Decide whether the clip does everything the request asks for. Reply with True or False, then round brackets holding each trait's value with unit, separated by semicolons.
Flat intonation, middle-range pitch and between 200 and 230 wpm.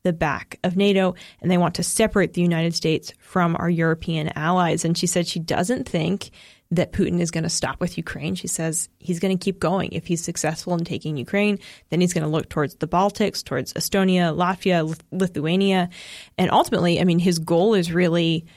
True (2.1 semitones; 175 Hz; 205 wpm)